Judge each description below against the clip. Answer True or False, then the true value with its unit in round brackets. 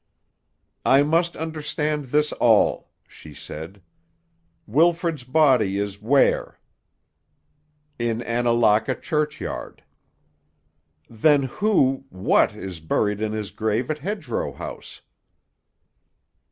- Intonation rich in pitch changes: True (6.1 semitones)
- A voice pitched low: True (130 Hz)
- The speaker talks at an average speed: False (85 wpm)